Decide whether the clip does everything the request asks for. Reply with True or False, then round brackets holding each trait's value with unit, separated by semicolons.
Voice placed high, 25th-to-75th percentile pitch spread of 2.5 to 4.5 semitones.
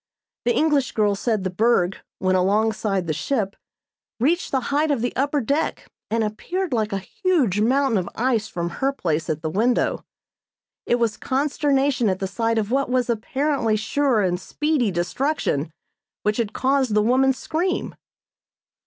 False (235 Hz; 5.3 semitones)